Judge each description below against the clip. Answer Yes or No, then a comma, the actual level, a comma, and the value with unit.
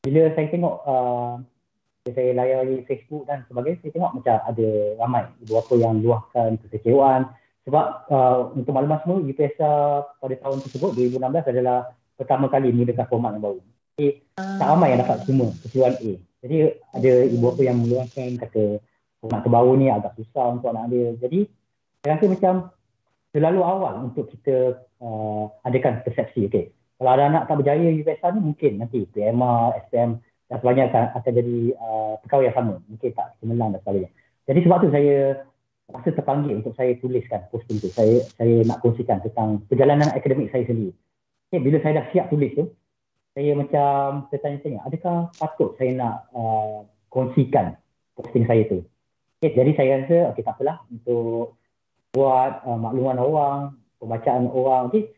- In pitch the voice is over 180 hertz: No, low, 130 Hz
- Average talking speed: No, fast, 165 wpm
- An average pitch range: Yes, average, 3.5 semitones